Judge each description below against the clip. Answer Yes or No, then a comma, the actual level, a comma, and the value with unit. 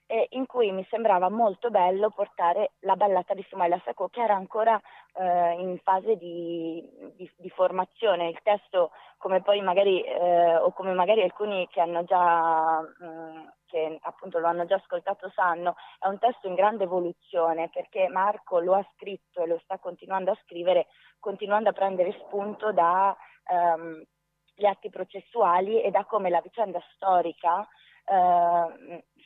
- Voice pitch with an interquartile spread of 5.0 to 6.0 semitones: No, narrow, 2.5 semitones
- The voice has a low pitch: No, medium, 185 Hz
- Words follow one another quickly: No, average, 155 wpm